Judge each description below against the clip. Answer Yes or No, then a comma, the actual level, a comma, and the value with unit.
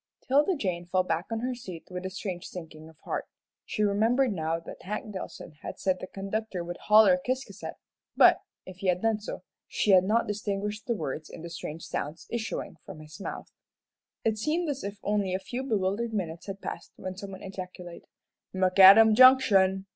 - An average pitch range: Yes, average, 3.4 semitones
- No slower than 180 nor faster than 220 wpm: Yes, average, 185 wpm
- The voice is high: Yes, high, 195 Hz